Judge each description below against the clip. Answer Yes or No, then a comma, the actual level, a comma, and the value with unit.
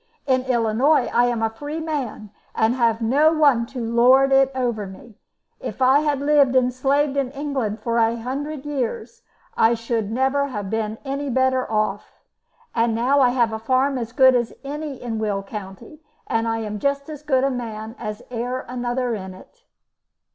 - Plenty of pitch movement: No, average, 3.5 semitones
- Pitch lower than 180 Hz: No, very high, 250 Hz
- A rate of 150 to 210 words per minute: Yes, average, 180 wpm